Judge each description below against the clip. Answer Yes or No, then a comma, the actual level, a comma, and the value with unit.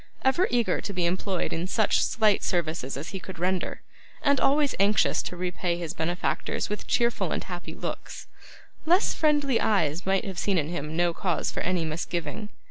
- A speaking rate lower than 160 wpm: No, average, 180 wpm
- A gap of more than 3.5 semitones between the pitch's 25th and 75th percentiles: Yes, average, 4.2 semitones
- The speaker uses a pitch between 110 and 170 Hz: No, medium, 185 Hz